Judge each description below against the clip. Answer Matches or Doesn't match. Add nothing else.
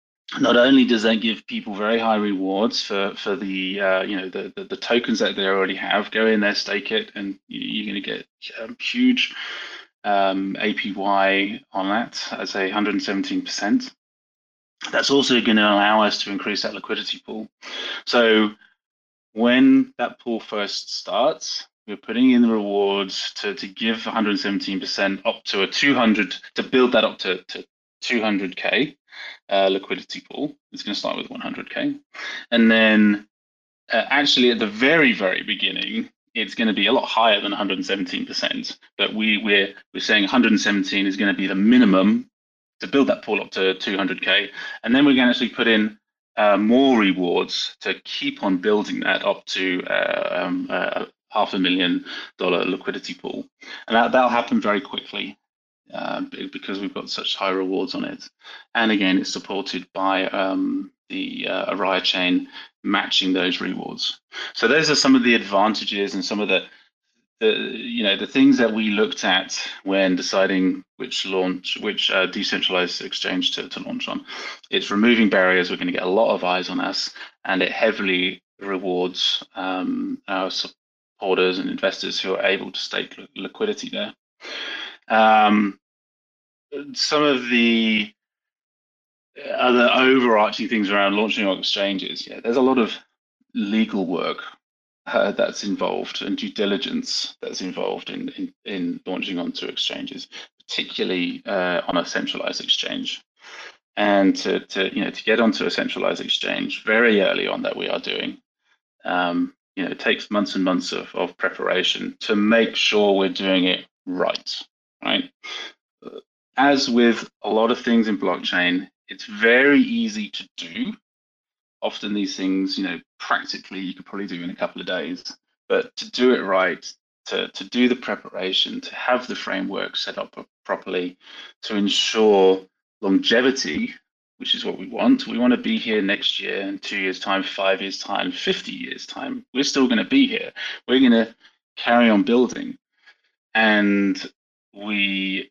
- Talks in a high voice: Doesn't match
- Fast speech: Doesn't match